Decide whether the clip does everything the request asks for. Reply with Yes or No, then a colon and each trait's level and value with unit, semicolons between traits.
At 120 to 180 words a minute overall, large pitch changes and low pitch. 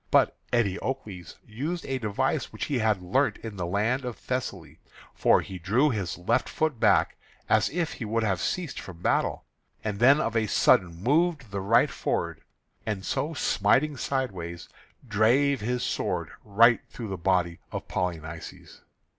Yes: average, 165 wpm; wide, 5.7 semitones; low, 110 Hz